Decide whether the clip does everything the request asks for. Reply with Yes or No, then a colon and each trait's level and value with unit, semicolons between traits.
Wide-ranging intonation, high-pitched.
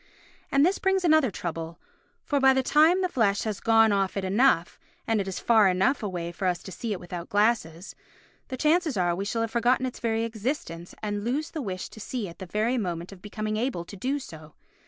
Yes: wide, 5.9 semitones; high, 215 Hz